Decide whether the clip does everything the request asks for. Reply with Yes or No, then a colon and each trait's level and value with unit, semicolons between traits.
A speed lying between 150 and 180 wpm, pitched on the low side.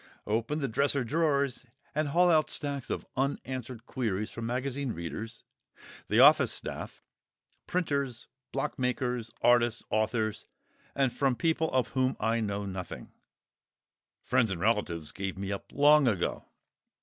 No: slow, 135 wpm; low, 125 Hz